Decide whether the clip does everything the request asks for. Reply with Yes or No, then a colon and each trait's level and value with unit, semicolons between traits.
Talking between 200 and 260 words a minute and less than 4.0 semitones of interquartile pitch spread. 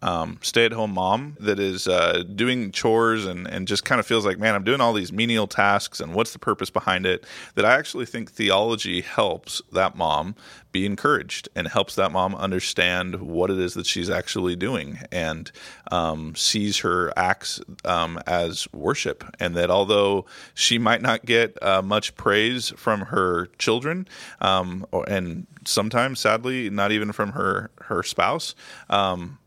No: average, 170 wpm; average, 3.6 semitones